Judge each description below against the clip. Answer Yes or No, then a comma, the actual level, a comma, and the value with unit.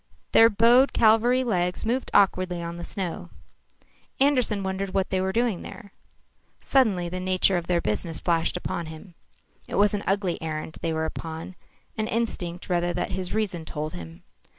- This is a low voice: No, medium, 185 Hz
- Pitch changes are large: No, average, 4.0 semitones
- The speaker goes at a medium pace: Yes, average, 170 wpm